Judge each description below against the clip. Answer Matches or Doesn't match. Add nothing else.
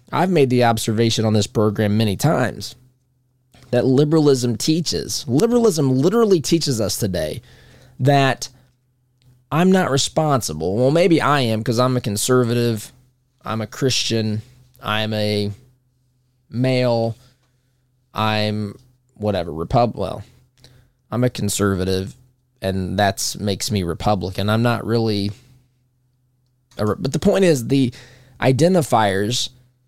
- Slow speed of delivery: Matches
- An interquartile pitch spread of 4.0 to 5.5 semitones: Doesn't match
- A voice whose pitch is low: Matches